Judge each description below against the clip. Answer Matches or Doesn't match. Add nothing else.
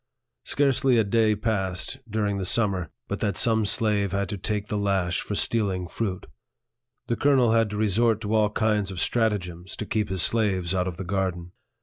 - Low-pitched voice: Matches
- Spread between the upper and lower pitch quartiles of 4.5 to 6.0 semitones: Doesn't match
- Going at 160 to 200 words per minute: Matches